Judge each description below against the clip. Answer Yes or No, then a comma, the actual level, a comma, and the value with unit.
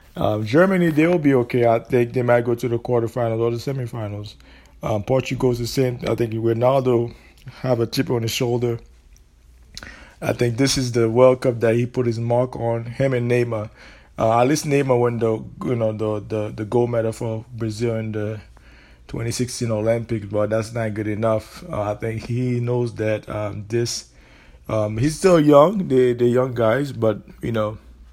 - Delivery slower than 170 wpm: No, average, 190 wpm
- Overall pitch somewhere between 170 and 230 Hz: No, low, 115 Hz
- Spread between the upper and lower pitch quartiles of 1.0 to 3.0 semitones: Yes, narrow, 2.5 semitones